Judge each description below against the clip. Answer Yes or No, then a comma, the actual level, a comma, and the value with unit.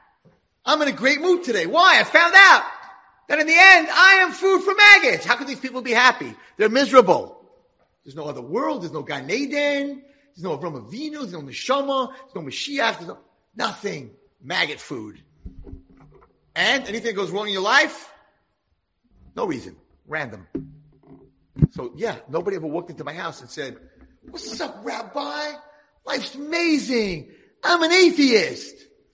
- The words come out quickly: No, average, 165 wpm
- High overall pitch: Yes, very high, 275 Hz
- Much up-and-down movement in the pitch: Yes, wide, 6.3 semitones